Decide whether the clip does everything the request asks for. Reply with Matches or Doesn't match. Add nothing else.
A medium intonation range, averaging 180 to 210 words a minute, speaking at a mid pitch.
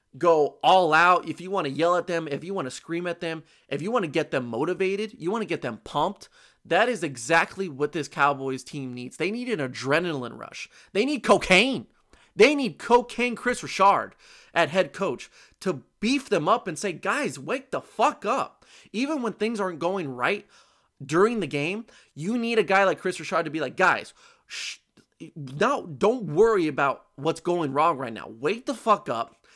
Doesn't match